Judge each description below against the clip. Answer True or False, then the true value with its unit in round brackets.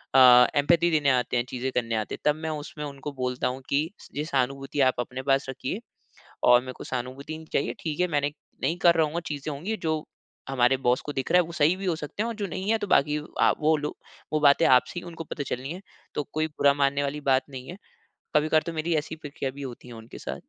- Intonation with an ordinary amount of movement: True (3.4 semitones)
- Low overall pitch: False (145 Hz)